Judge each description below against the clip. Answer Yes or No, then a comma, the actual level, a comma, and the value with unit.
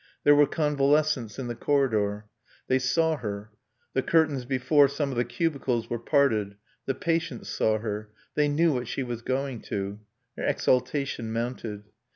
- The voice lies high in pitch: No, low, 130 Hz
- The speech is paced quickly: No, average, 160 wpm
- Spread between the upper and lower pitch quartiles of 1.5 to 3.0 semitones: No, average, 4.3 semitones